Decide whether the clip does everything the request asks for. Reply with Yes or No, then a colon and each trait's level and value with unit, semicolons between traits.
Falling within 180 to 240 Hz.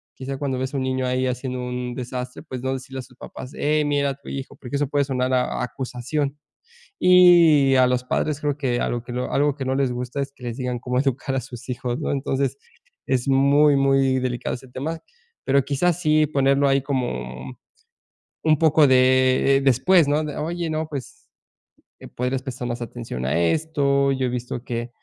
No: low, 135 Hz